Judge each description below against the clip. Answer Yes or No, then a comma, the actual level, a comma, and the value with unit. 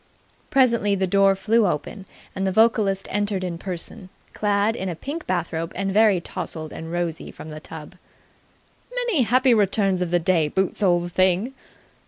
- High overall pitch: Yes, high, 195 Hz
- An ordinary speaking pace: Yes, average, 165 wpm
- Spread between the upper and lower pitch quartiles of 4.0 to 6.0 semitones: No, average, 3.6 semitones